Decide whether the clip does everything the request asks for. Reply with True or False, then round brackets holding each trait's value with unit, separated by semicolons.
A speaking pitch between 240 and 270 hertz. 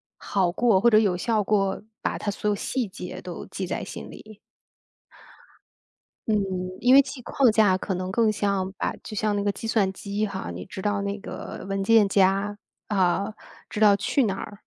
False (205 Hz)